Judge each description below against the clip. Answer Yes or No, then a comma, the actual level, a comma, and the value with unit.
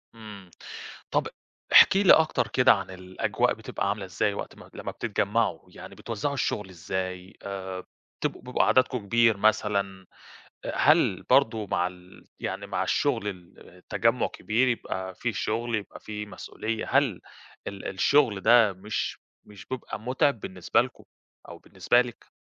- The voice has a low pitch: Yes, low, 105 Hz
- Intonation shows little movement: No, average, 3.8 semitones